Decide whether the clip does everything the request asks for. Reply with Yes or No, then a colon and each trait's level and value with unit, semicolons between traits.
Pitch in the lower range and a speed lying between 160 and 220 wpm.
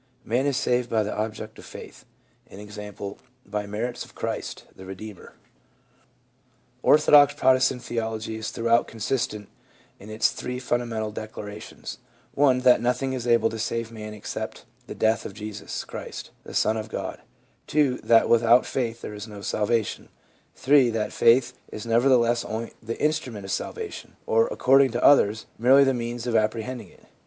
Yes: low, 115 Hz; average, 165 wpm